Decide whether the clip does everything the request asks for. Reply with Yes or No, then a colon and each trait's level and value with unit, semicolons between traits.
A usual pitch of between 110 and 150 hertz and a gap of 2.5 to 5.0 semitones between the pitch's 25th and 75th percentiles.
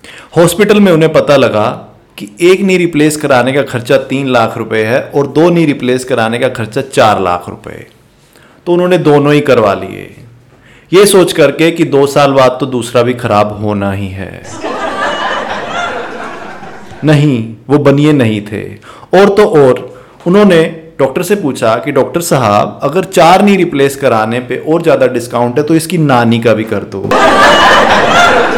No: medium, 140 Hz; wide, 5.5 semitones